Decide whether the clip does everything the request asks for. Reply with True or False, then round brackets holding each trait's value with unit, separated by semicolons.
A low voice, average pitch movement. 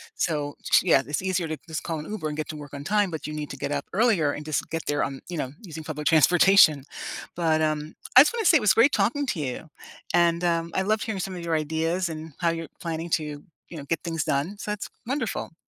False (165 Hz; 3.7 semitones)